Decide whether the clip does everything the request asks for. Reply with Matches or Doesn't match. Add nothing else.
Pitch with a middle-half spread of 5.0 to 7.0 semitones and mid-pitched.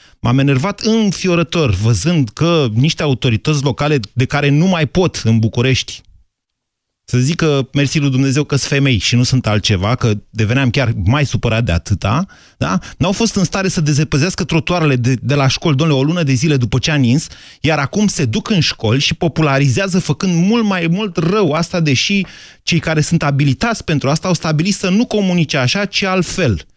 Matches